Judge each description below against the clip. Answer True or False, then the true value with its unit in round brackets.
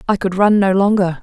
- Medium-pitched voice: False (195 Hz)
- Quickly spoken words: True (245 wpm)